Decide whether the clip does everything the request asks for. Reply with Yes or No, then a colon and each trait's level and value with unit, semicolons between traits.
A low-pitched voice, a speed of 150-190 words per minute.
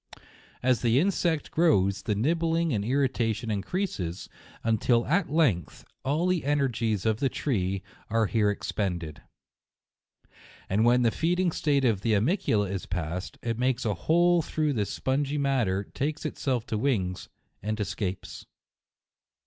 No: low, 120 Hz; average, 140 wpm